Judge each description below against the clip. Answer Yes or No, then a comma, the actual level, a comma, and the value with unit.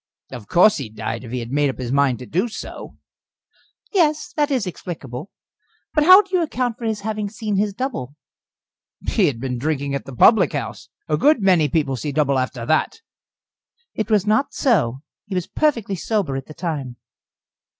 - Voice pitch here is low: No, medium, 165 Hz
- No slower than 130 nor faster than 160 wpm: No, average, 190 wpm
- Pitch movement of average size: No, wide, 8.6 semitones